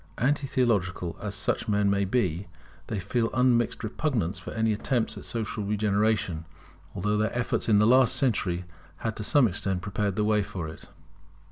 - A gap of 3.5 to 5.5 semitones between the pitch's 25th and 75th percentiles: No, average, 3.0 semitones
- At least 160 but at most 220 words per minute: Yes, average, 170 wpm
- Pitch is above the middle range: No, low, 105 Hz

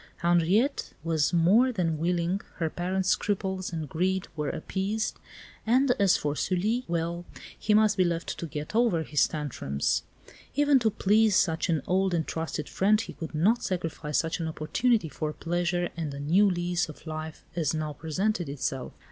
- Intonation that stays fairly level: No, average, 3.9 semitones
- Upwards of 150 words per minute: Yes, average, 170 wpm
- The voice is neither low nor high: Yes, medium, 175 Hz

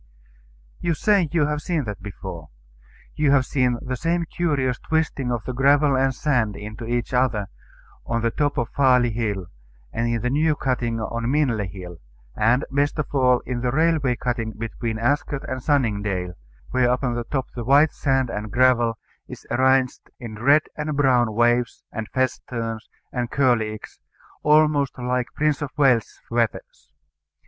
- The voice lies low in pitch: Yes, low, 125 Hz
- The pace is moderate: Yes, average, 160 wpm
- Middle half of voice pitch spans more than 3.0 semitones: Yes, average, 3.6 semitones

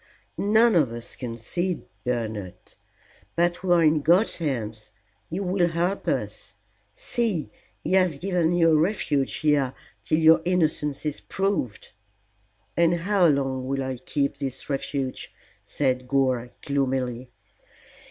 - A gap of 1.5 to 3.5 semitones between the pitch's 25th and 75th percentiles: No, average, 5.1 semitones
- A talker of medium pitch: Yes, medium, 150 Hz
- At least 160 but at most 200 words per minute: No, slow, 135 wpm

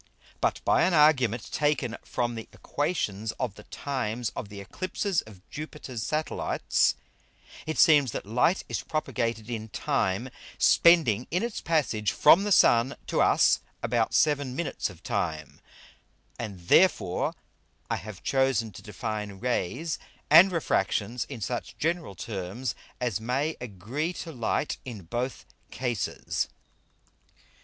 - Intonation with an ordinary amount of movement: No, wide, 5.9 semitones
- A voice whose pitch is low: Yes, low, 125 Hz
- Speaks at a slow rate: Yes, slow, 130 wpm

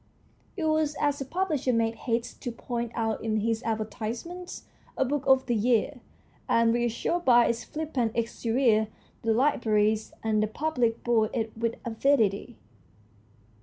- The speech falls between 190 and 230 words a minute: No, average, 145 wpm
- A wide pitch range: No, average, 3.3 semitones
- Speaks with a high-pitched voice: Yes, high, 235 Hz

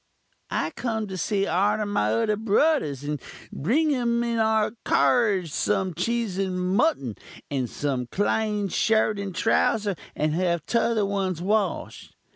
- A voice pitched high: Yes, high, 200 Hz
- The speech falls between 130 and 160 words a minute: Yes, average, 140 wpm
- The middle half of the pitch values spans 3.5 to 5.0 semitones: Yes, average, 4.3 semitones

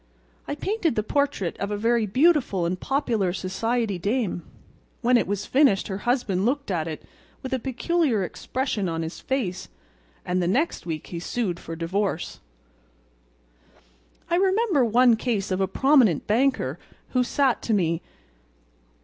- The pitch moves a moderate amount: No, wide, 6.1 semitones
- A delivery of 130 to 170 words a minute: Yes, average, 150 wpm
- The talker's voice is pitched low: No, high, 220 Hz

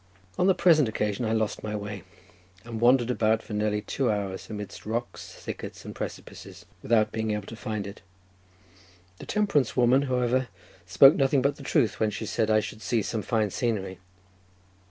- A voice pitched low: Yes, low, 110 Hz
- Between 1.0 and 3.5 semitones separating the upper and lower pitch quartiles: Yes, average, 3.1 semitones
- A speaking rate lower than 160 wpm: No, average, 175 wpm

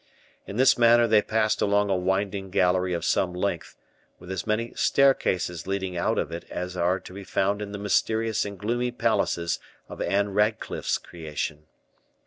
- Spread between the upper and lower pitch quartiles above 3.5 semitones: No, average, 3.2 semitones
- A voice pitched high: No, low, 100 Hz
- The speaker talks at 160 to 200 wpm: Yes, average, 170 wpm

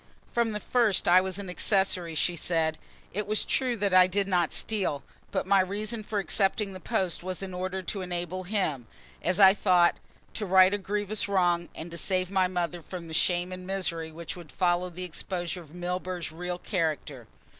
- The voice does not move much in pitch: Yes, narrow, 2.1 semitones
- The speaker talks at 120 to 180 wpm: No, average, 195 wpm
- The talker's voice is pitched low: No, medium, 185 Hz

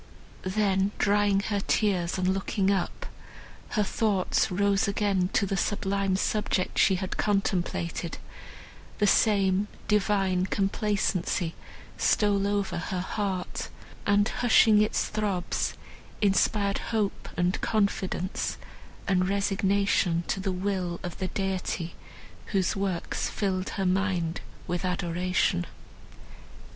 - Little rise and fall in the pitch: Yes, narrow, 1.8 semitones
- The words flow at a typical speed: No, slow, 110 wpm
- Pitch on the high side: Yes, high, 195 Hz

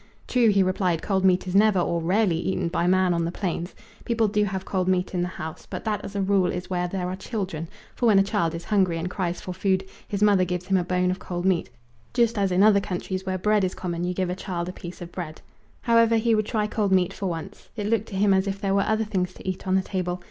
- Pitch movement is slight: Yes, narrow, 2.2 semitones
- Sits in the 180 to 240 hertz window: Yes, high, 190 Hz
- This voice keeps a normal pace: No, fast, 270 wpm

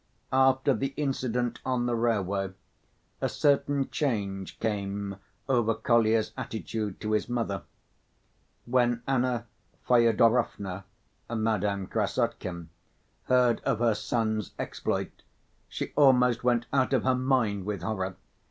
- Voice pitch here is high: No, low, 115 Hz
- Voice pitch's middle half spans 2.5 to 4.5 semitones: Yes, average, 3.6 semitones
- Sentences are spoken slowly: Yes, slow, 115 wpm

